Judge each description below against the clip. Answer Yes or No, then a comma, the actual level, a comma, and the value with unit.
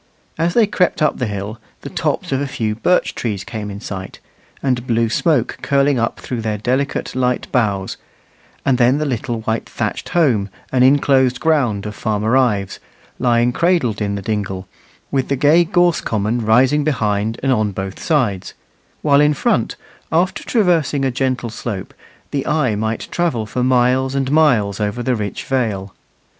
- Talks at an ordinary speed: Yes, average, 170 wpm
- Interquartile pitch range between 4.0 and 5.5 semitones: Yes, average, 4.7 semitones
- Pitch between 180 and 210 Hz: No, low, 125 Hz